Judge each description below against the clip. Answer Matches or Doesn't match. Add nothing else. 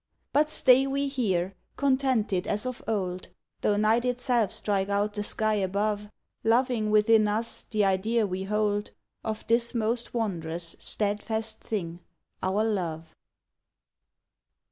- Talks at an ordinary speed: Doesn't match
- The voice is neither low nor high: Doesn't match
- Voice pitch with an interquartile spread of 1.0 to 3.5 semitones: Matches